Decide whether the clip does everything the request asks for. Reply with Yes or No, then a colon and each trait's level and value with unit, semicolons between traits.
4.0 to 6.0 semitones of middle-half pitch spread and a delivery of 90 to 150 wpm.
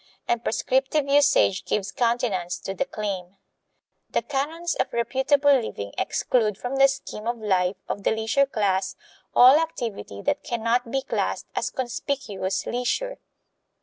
Yes: average, 5.3 semitones; average, 145 wpm